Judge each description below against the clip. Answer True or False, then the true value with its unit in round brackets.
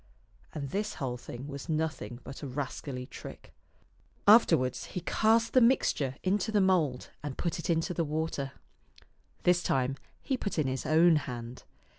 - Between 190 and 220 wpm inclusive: False (160 wpm)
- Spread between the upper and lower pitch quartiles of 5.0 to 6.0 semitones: True (5.4 semitones)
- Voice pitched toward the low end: False (155 Hz)